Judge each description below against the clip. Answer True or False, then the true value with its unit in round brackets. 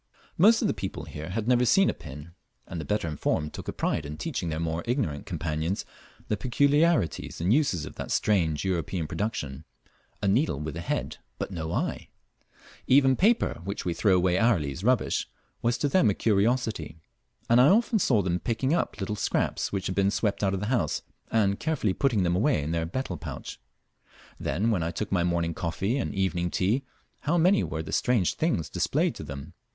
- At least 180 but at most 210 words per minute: True (200 wpm)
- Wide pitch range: True (6.8 semitones)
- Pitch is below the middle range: True (95 Hz)